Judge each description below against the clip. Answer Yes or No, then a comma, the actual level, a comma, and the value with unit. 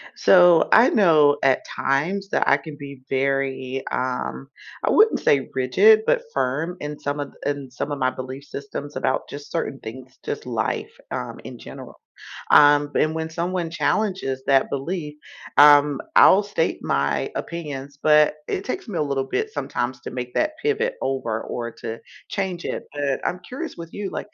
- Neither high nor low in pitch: Yes, medium, 145 Hz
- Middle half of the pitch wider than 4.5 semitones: Yes, average, 4.9 semitones